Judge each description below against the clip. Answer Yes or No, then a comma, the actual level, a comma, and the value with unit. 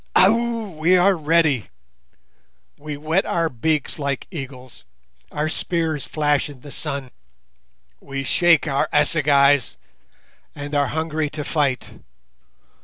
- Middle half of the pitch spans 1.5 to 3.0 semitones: Yes, average, 2.7 semitones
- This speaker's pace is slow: Yes, slow, 115 wpm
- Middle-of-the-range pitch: Yes, medium, 150 Hz